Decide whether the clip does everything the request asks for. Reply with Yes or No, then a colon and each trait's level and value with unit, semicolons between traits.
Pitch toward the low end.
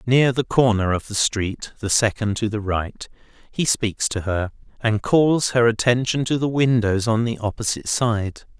Yes: low, 115 Hz